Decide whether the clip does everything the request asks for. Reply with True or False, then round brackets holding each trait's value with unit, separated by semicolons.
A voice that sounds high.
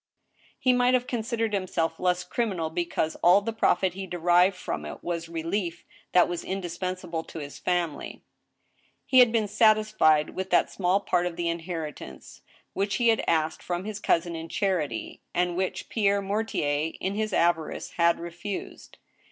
False (180 Hz)